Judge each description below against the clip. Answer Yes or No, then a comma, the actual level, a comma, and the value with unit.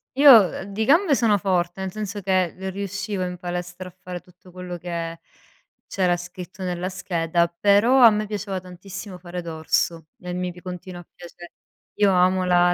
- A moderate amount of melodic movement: No, narrow, 2.1 semitones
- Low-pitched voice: No, medium, 180 Hz